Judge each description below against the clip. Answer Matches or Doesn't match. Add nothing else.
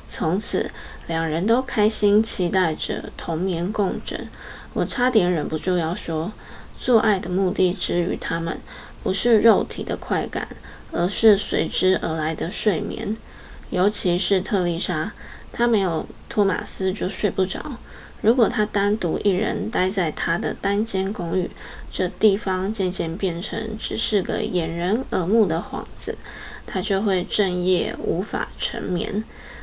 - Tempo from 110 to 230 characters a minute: Matches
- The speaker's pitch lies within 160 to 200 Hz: Matches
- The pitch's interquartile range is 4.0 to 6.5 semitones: Doesn't match